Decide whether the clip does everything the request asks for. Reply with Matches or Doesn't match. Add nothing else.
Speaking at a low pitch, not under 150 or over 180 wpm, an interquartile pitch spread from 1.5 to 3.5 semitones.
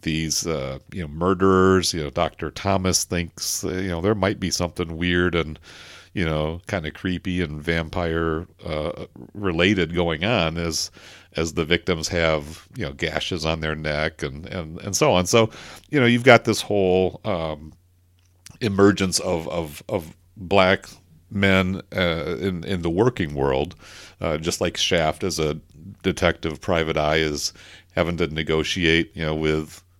Matches